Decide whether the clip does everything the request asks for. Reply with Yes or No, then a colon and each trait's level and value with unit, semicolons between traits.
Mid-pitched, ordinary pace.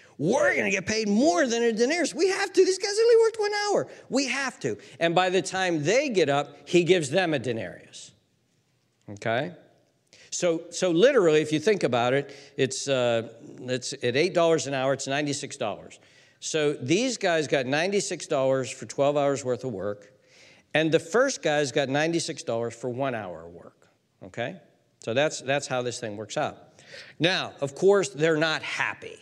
Yes: medium, 150 Hz; average, 180 wpm